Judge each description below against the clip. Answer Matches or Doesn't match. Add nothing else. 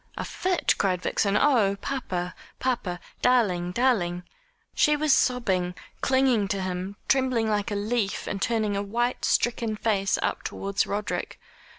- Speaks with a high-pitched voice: Matches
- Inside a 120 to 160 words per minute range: Matches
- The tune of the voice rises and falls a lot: Doesn't match